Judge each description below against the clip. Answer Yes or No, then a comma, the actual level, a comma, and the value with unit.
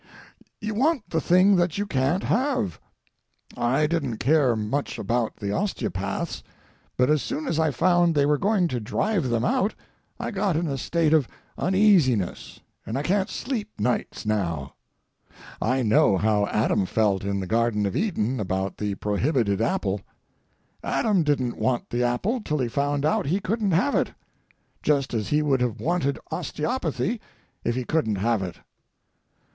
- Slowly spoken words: No, average, 160 wpm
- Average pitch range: No, wide, 8.3 semitones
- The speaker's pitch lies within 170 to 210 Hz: No, medium, 140 Hz